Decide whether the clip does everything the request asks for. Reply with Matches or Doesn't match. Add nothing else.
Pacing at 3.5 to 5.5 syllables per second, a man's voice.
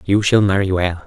Matches